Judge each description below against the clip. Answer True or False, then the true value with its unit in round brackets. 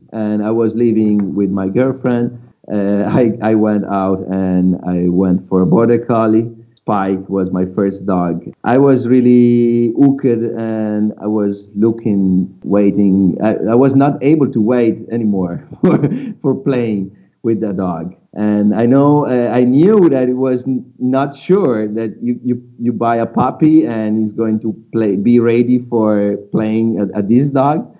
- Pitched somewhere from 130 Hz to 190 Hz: False (110 Hz)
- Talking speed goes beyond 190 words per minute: False (170 wpm)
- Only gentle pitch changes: False (3.3 semitones)